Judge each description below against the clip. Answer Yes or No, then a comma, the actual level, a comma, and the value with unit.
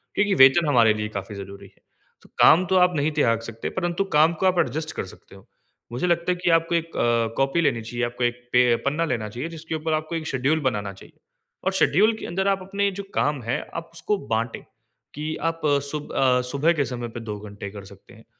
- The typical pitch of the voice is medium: Yes, medium, 145 Hz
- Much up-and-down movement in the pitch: Yes, wide, 6.3 semitones